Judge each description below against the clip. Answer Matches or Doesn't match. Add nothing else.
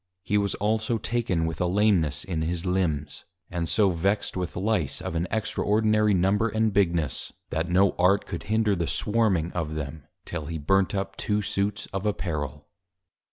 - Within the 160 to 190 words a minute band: Matches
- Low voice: Matches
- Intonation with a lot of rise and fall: Doesn't match